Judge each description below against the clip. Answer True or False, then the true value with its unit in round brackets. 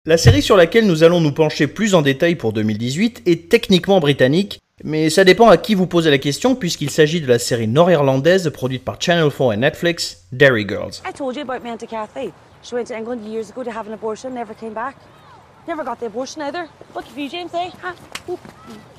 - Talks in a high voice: False (180 Hz)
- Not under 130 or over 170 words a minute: False (195 wpm)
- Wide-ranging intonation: True (7.9 semitones)